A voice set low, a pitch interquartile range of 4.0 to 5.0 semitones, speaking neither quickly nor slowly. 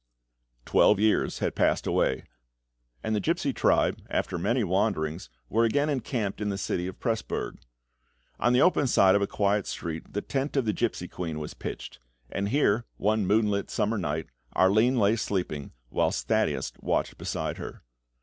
No: low, 105 Hz; average, 3.6 semitones; average, 165 wpm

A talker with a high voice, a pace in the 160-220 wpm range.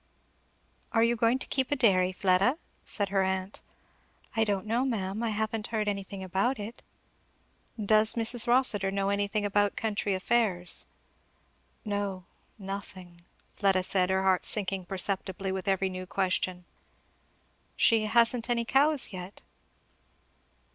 No: high, 200 Hz; slow, 135 wpm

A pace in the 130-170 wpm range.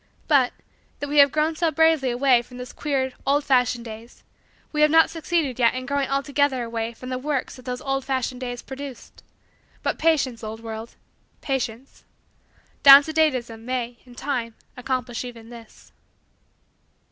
Yes: average, 165 wpm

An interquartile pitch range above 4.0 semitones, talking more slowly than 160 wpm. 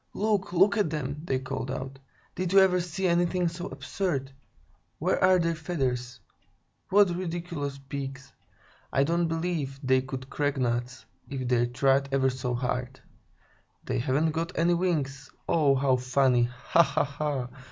Yes: average, 4.7 semitones; average, 150 wpm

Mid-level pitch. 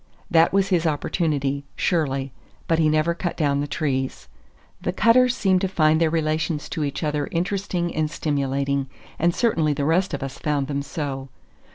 Yes: medium, 155 Hz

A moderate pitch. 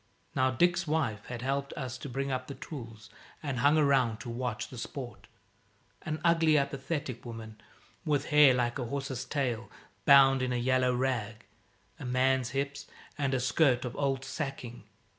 No: low, 130 Hz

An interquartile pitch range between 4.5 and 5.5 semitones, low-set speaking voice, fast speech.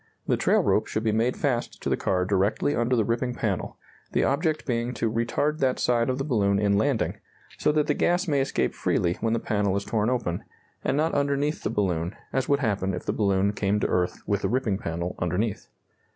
Yes: average, 5.1 semitones; low, 115 Hz; fast, 220 wpm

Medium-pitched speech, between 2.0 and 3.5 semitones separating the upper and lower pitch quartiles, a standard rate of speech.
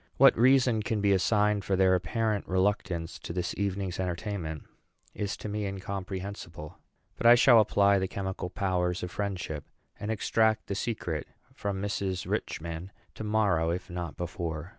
No: very low, 95 Hz; average, 2.7 semitones; average, 155 wpm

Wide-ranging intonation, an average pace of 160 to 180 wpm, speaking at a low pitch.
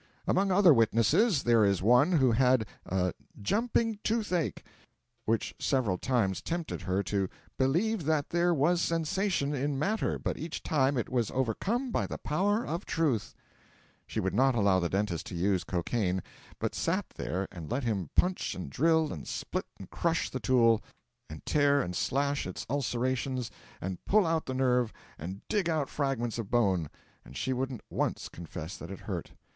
Yes: wide, 8.1 semitones; average, 170 wpm; low, 130 Hz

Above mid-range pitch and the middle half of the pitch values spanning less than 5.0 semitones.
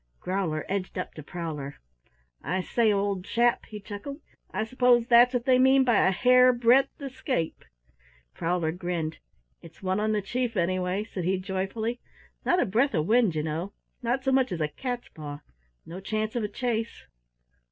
No: high, 210 Hz; average, 5.3 semitones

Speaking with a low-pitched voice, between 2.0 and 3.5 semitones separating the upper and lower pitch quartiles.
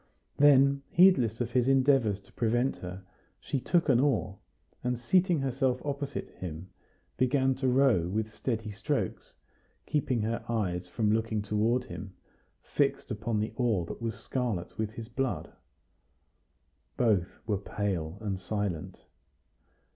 No: low, 115 Hz; average, 4.3 semitones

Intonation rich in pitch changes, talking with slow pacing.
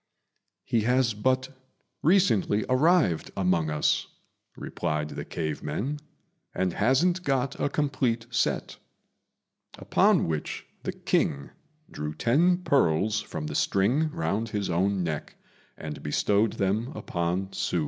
Yes: wide, 7.4 semitones; slow, 120 wpm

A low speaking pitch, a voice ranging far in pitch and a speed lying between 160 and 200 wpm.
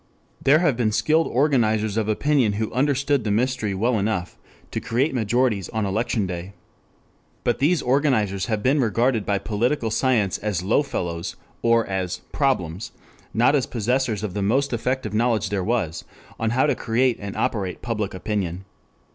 No: low, 110 Hz; average, 4.1 semitones; average, 165 wpm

